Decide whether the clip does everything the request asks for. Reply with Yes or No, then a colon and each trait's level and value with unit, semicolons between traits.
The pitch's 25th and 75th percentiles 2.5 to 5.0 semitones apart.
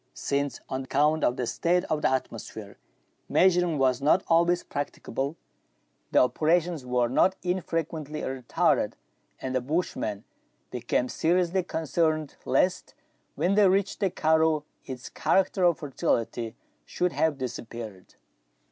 No: wide, 5.4 semitones